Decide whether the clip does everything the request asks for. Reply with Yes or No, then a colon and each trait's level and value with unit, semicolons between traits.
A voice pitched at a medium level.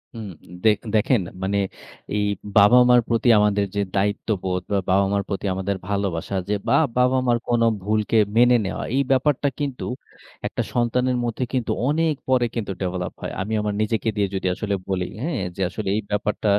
No: low, 105 Hz